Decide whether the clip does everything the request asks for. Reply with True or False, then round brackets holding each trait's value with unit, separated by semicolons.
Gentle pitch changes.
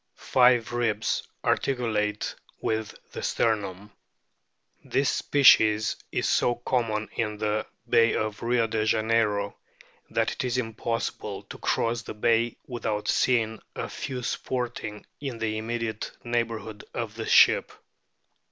True (1.8 semitones)